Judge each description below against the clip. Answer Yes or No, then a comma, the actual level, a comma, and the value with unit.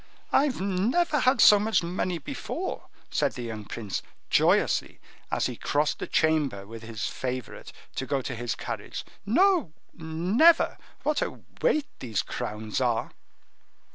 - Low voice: No, medium, 160 Hz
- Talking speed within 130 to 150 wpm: Yes, average, 140 wpm